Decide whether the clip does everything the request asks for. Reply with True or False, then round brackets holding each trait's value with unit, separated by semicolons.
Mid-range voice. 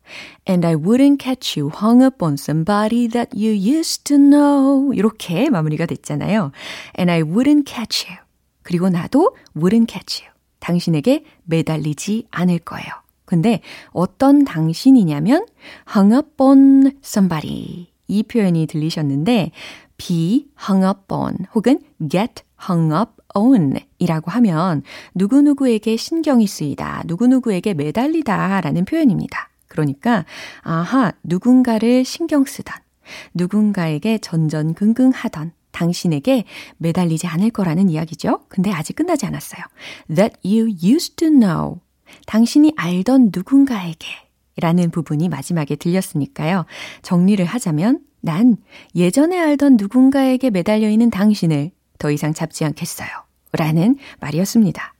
False (205 Hz)